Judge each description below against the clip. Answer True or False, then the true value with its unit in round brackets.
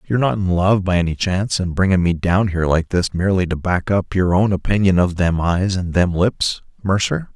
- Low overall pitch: True (90 Hz)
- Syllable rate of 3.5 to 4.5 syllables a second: False (5.4 syllables/s)